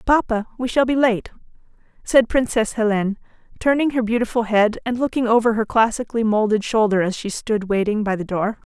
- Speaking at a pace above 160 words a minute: Yes, average, 180 wpm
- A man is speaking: No, female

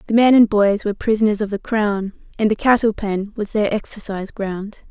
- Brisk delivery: Yes, fast, 210 wpm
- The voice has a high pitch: Yes, high, 210 Hz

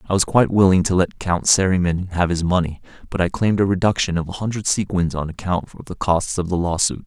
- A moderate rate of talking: No, fast, 240 wpm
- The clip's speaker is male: Yes, male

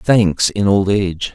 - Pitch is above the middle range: No, low, 100 Hz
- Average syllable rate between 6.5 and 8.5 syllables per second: No, 3.8 syllables/s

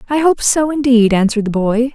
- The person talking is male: No, female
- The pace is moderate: No, fast, 215 wpm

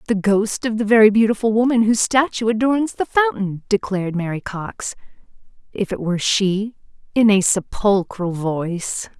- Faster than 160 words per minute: No, average, 150 wpm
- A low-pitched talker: No, high, 210 Hz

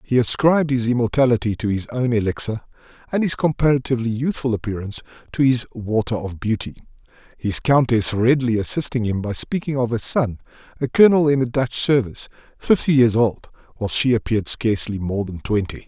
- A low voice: Yes, low, 120 Hz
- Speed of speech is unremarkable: Yes, average, 165 wpm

